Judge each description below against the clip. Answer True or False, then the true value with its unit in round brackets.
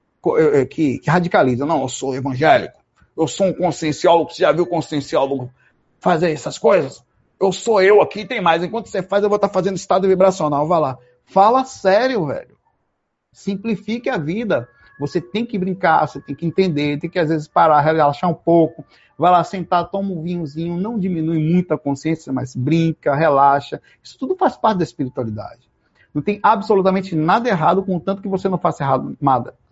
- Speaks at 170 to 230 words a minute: True (180 wpm)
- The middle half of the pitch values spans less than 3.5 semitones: False (4.5 semitones)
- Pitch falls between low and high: True (170 Hz)